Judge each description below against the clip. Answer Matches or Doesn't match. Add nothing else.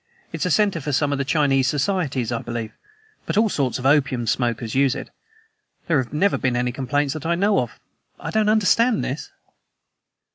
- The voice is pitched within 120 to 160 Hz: Matches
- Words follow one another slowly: Doesn't match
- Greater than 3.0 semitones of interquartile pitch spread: Matches